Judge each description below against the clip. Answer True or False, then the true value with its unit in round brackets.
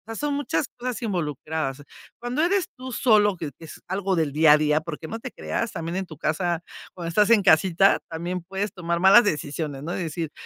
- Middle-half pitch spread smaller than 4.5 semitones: False (5.2 semitones)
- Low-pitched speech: False (175 Hz)